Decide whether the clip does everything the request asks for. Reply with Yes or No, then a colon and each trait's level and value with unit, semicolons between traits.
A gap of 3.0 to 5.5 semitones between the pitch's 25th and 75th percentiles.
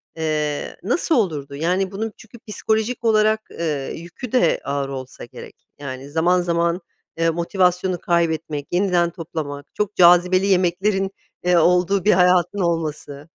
Yes: average, 3.5 semitones